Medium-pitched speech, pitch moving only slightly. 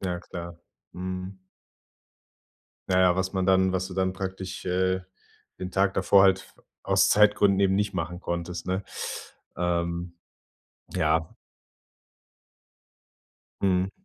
No: very low, 95 Hz; narrow, 1.3 semitones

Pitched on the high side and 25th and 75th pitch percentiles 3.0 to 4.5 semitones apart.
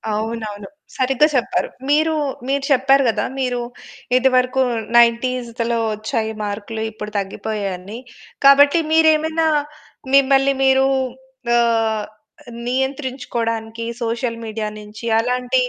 Yes: high, 240 Hz; average, 3.3 semitones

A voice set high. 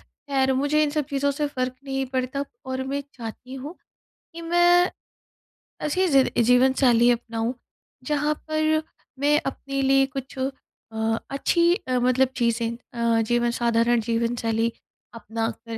Yes: very high, 265 Hz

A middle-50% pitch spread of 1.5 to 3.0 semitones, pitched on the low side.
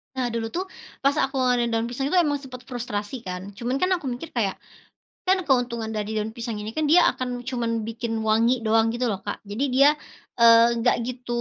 No: narrow, 2.4 semitones; high, 240 Hz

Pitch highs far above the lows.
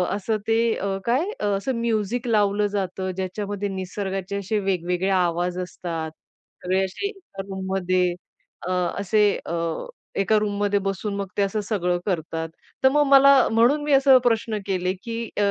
No: average, 3.2 semitones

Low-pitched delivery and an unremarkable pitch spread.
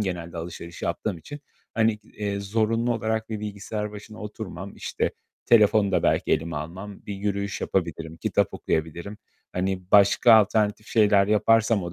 Yes: low, 100 Hz; average, 3.1 semitones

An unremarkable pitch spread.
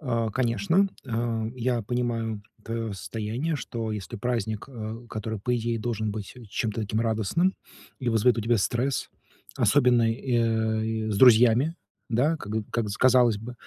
No: narrow, 2.0 semitones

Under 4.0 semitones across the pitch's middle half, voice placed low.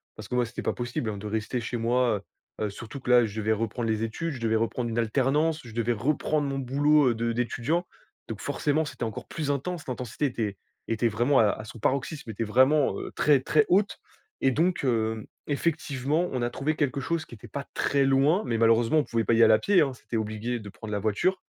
No: average, 4.3 semitones; low, 125 Hz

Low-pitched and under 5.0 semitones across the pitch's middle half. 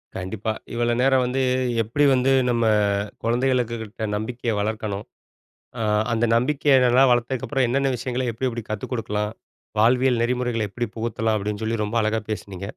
Yes: low, 115 Hz; narrow, 2.5 semitones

